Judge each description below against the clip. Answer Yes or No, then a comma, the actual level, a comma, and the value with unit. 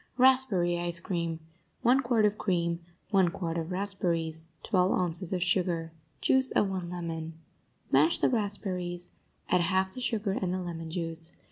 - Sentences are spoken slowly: No, average, 155 wpm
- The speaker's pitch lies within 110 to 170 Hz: No, medium, 180 Hz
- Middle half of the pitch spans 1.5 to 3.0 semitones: Yes, average, 2.7 semitones